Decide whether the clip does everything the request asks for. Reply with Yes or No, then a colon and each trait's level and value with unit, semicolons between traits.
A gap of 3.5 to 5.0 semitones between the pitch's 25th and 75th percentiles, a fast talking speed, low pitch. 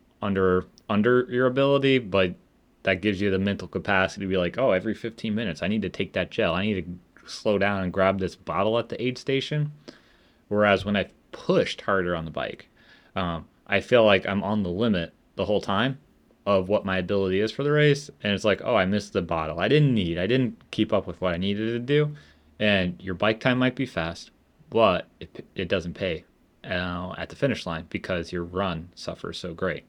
Yes: average, 4.3 semitones; fast, 215 wpm; low, 100 Hz